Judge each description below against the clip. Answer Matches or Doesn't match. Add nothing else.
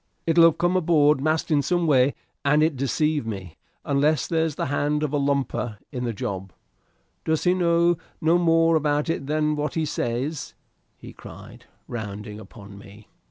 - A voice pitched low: Doesn't match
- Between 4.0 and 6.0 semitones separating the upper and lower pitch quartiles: Matches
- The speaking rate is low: Doesn't match